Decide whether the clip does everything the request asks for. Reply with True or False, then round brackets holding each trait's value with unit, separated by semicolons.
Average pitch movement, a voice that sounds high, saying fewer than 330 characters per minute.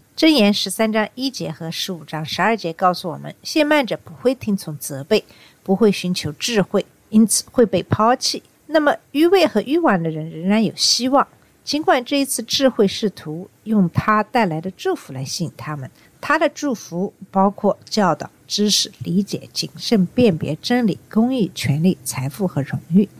False (6.4 semitones; 200 Hz; 260 characters per minute)